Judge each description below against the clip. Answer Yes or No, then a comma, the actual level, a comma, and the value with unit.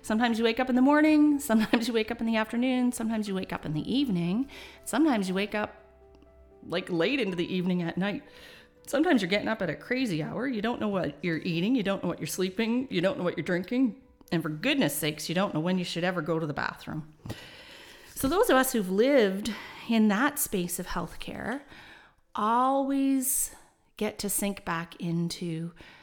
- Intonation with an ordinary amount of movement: No, wide, 6.1 semitones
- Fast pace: Yes, fast, 210 wpm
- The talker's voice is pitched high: Yes, high, 205 Hz